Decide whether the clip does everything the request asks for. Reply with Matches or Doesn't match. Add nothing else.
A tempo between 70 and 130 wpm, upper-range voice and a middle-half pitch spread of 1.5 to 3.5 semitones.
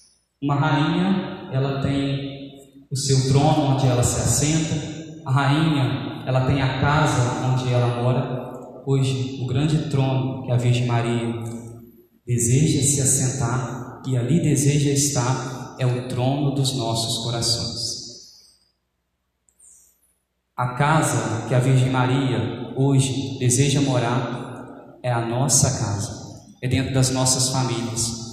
Doesn't match